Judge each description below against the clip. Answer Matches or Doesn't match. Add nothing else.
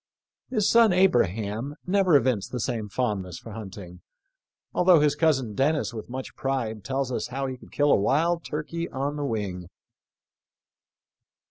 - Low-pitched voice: Matches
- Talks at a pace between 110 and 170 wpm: Matches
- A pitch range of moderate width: Doesn't match